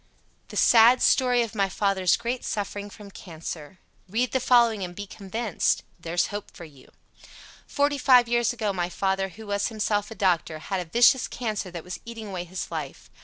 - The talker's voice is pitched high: Yes, high, 205 Hz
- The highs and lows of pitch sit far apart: No, average, 4.4 semitones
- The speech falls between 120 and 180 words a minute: No, average, 190 wpm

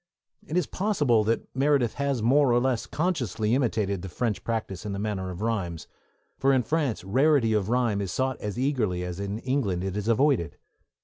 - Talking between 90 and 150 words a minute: No, average, 190 wpm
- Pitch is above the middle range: No, low, 115 Hz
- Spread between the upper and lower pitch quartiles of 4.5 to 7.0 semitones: Yes, average, 5.2 semitones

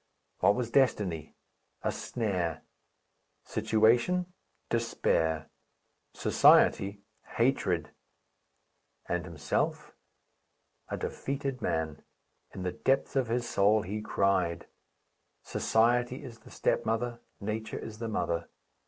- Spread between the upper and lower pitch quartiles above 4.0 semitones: Yes, average, 5.0 semitones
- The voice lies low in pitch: Yes, low, 110 Hz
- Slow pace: Yes, slow, 95 wpm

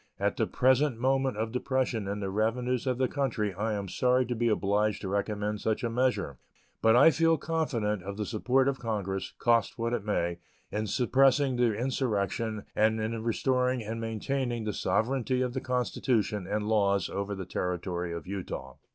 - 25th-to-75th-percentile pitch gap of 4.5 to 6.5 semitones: No, average, 3.8 semitones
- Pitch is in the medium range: No, low, 110 Hz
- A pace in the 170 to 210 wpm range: Yes, average, 180 wpm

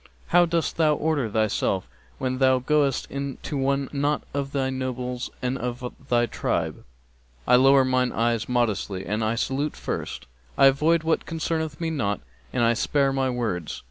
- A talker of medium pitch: No, low, 130 Hz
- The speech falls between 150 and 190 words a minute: Yes, average, 165 wpm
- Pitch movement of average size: Yes, average, 3.0 semitones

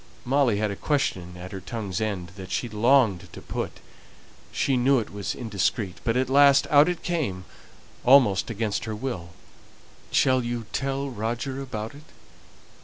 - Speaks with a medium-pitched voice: No, low, 115 Hz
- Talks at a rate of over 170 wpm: No, average, 160 wpm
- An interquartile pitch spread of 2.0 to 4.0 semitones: No, average, 5.0 semitones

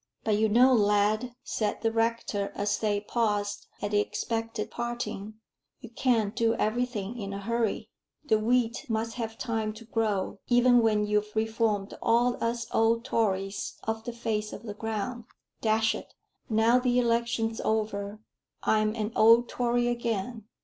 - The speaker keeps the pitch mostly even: Yes, narrow, 2.0 semitones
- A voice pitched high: Yes, high, 225 Hz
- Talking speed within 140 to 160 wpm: Yes, average, 155 wpm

